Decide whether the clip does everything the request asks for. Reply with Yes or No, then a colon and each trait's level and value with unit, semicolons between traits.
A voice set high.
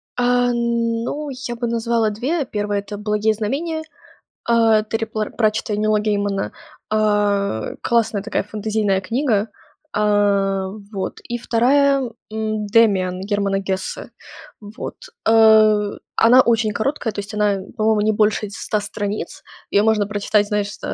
Yes: high, 215 Hz